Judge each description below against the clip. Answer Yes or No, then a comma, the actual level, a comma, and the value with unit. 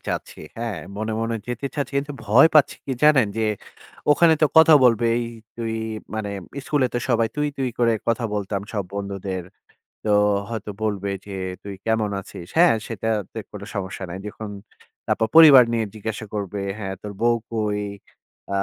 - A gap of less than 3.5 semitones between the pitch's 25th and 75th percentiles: Yes, average, 3.1 semitones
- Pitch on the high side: No, low, 110 Hz